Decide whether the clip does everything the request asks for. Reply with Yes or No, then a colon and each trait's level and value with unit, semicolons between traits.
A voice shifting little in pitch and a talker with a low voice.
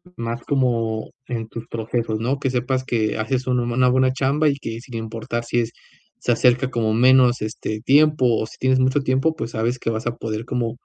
Yes: narrow, 2.3 semitones; low, 120 Hz